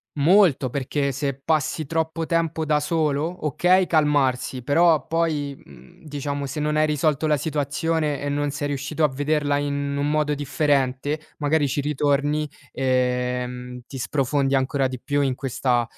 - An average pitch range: No, narrow, 2.1 semitones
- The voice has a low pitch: No, medium, 145 Hz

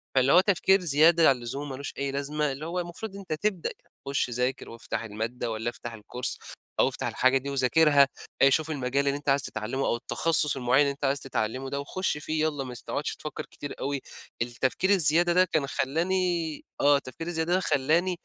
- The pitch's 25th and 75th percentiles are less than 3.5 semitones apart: No, average, 3.8 semitones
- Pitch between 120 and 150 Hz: Yes, medium, 140 Hz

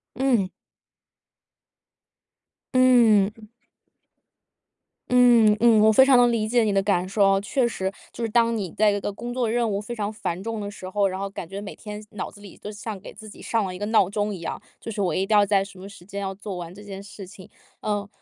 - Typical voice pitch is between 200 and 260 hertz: Yes, high, 205 Hz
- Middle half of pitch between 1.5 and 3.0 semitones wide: Yes, narrow, 2.5 semitones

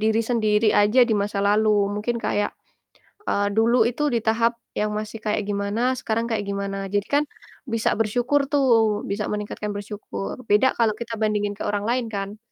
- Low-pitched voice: No, high, 215 Hz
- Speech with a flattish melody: Yes, narrow, 2.1 semitones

